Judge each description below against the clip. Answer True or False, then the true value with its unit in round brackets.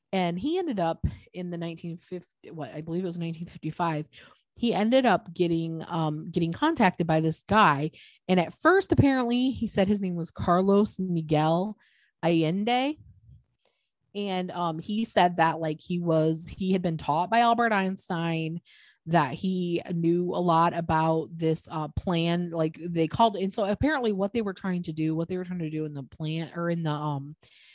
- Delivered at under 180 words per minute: False (185 wpm)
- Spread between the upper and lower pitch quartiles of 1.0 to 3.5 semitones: True (3.1 semitones)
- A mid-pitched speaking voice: True (170 Hz)